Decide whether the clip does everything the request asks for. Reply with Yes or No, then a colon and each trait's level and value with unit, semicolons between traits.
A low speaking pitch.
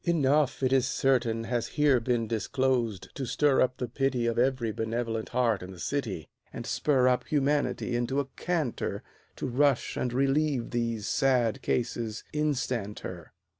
Yes: low, 125 Hz